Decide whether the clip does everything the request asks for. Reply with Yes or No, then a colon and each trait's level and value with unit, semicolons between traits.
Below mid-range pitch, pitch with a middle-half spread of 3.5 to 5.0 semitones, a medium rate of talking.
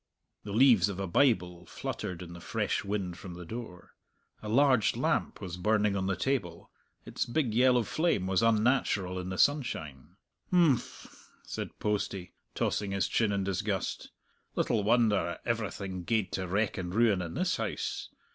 Yes: low, 100 Hz; average, 4.1 semitones; average, 160 wpm